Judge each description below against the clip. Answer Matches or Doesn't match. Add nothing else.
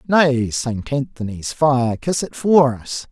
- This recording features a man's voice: Matches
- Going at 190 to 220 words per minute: Doesn't match